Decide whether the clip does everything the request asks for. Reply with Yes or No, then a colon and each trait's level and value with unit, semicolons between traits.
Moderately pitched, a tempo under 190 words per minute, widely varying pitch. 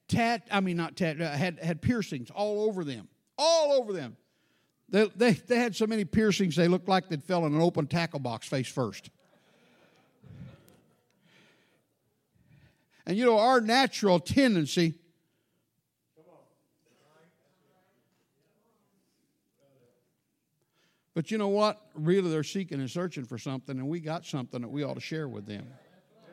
Yes: medium, 170 Hz; average, 140 wpm; wide, 6.1 semitones